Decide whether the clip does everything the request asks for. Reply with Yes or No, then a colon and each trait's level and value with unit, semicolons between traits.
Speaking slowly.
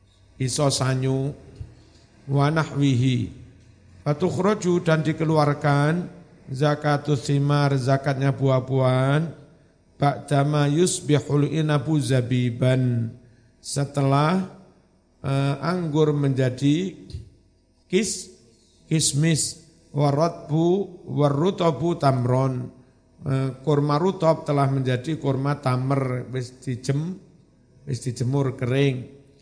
Yes: slow, 65 wpm